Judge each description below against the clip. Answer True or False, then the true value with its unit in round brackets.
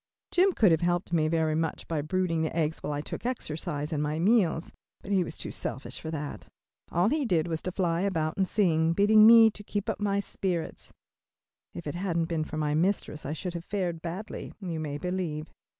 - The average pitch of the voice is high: False (170 Hz)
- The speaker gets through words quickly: True (215 wpm)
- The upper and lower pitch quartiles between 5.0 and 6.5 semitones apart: False (3.7 semitones)